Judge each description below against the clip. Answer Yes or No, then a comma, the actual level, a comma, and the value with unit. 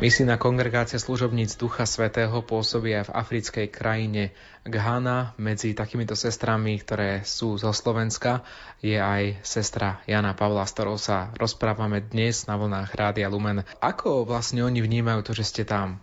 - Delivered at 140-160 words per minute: Yes, average, 145 wpm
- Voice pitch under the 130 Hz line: Yes, low, 110 Hz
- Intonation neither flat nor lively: No, narrow, 2.1 semitones